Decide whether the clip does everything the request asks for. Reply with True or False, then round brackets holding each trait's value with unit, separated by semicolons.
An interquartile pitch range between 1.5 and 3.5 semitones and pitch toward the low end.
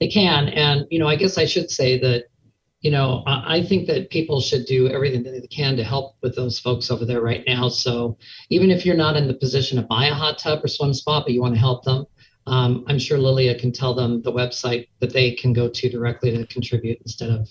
True (3.0 semitones; 130 Hz)